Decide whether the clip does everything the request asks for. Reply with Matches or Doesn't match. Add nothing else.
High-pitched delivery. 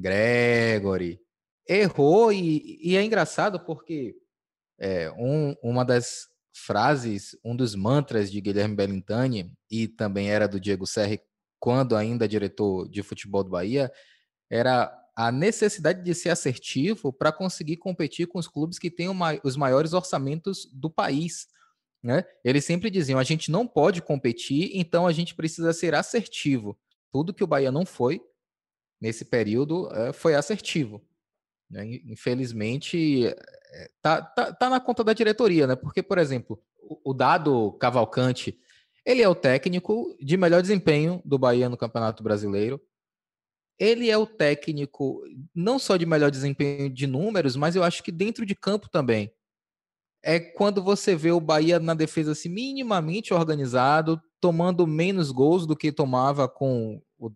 Doesn't match